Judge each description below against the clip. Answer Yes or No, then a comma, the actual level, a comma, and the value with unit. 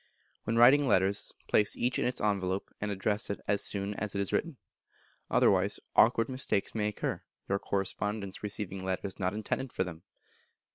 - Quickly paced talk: No, average, 175 wpm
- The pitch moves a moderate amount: No, narrow, 2.2 semitones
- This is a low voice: Yes, low, 105 Hz